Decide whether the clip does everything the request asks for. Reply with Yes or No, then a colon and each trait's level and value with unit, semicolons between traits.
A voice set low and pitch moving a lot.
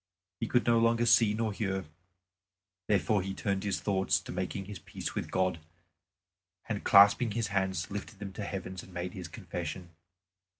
No: low, 100 Hz; narrow, 2.4 semitones